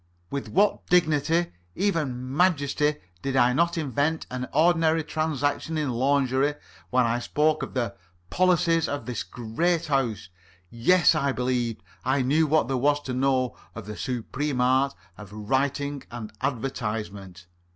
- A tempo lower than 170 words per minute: Yes, average, 140 wpm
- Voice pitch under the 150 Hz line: Yes, low, 135 Hz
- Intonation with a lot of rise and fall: No, average, 4.0 semitones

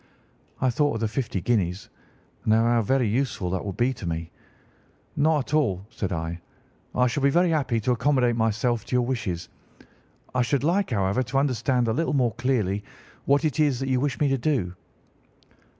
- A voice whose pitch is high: No, low, 125 Hz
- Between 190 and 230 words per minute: Yes, average, 195 wpm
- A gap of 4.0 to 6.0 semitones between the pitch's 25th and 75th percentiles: Yes, average, 4.5 semitones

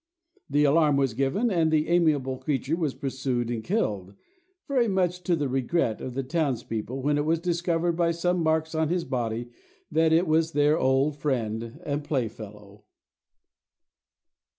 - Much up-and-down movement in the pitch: No, average, 4.5 semitones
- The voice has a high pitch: No, medium, 150 Hz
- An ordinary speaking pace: Yes, average, 150 wpm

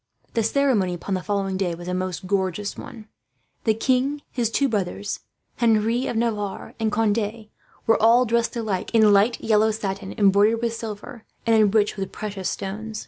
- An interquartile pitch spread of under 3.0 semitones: Yes, narrow, 2.5 semitones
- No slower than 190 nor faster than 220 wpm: No, average, 170 wpm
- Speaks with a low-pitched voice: No, high, 215 Hz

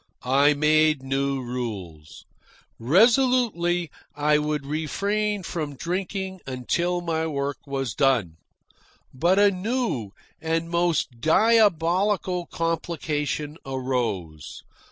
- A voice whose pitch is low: No, medium, 155 Hz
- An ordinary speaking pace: No, slow, 95 wpm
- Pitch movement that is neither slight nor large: Yes, average, 4.9 semitones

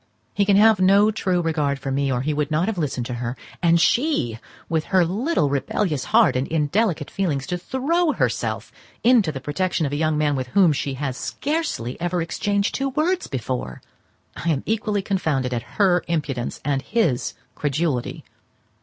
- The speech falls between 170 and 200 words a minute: Yes, average, 180 wpm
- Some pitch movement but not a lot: No, wide, 6.7 semitones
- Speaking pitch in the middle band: Yes, medium, 165 Hz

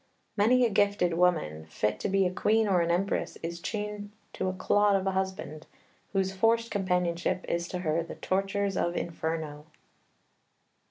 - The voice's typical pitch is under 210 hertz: Yes, medium, 185 Hz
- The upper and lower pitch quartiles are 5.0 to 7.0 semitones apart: No, average, 3.0 semitones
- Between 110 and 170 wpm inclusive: Yes, average, 165 wpm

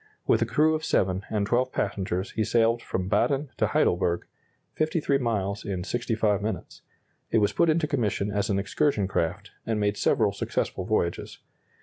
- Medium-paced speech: Yes, average, 165 wpm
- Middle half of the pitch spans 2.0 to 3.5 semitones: No, average, 4.3 semitones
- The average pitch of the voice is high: No, low, 105 Hz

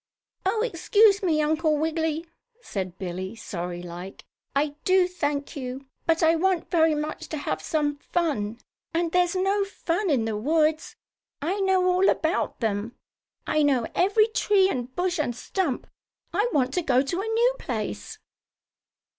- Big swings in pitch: Yes, wide, 6.4 semitones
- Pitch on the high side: Yes, very high, 315 Hz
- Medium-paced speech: Yes, average, 155 wpm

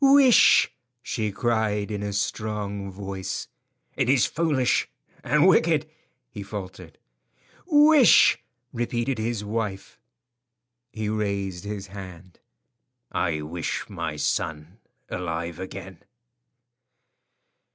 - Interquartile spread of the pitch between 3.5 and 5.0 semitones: Yes, average, 4.1 semitones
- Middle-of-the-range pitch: No, low, 105 Hz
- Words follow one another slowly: Yes, slow, 95 wpm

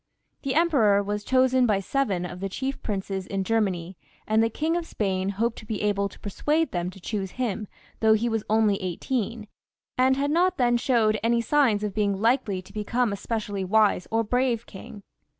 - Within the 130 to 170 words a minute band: No, average, 195 wpm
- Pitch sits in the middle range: No, high, 220 Hz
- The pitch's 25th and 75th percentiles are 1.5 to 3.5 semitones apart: No, average, 3.9 semitones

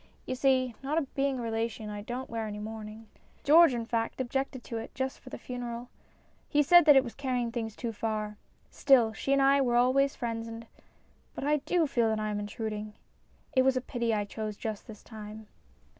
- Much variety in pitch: No, average, 3.3 semitones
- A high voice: Yes, high, 235 Hz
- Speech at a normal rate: No, fast, 210 wpm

